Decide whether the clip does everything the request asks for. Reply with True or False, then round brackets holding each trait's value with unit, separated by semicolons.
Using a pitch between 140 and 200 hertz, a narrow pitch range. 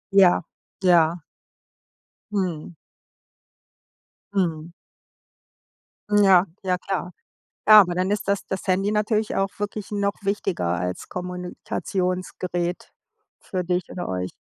True (185 Hz; 2.1 semitones)